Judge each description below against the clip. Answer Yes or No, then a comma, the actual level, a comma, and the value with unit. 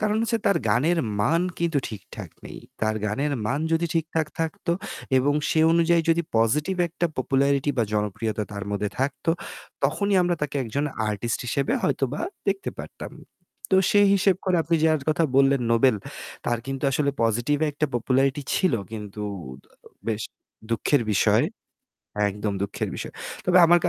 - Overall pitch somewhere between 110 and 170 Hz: Yes, medium, 140 Hz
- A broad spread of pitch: Yes, wide, 6.5 semitones